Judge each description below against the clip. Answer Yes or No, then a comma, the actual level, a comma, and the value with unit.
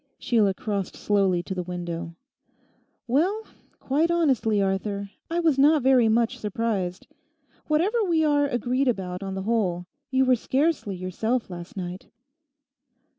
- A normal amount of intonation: No, wide, 6.3 semitones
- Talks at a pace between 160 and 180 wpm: No, slow, 135 wpm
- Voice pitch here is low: No, high, 225 Hz